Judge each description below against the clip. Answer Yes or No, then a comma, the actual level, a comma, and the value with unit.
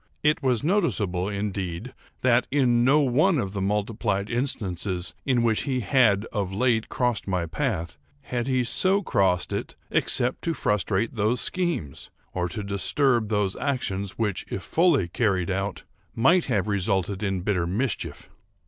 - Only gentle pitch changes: No, average, 4.9 semitones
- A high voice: No, low, 110 Hz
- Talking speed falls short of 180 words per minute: Yes, average, 150 wpm